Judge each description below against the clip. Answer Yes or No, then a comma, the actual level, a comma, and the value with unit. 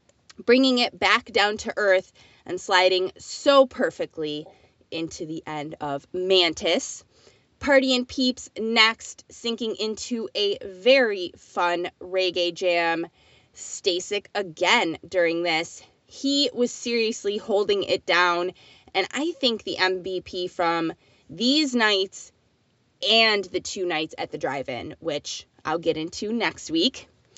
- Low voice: No, high, 190 Hz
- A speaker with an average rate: No, slow, 125 wpm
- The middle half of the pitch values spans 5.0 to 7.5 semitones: Yes, average, 5.3 semitones